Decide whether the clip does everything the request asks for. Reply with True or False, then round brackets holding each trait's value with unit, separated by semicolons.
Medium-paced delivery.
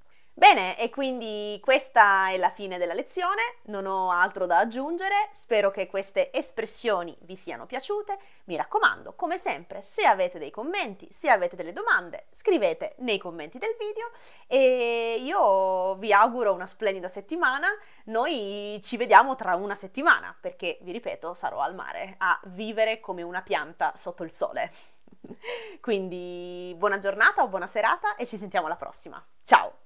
True (155 wpm)